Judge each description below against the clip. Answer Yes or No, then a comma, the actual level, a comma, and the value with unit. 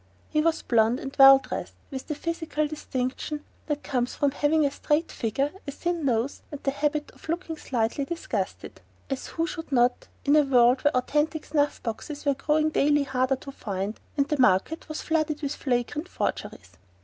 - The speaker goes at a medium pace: Yes, average, 185 wpm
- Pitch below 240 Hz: No, very high, 285 Hz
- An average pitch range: Yes, average, 3.0 semitones